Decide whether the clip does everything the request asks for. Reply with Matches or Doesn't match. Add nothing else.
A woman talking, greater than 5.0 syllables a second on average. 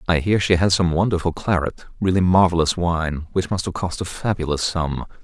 Doesn't match